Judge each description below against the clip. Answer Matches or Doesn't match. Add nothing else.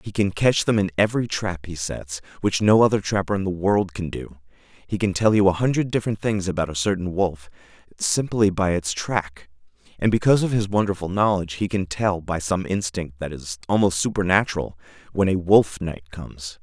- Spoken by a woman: Doesn't match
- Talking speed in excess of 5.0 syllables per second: Matches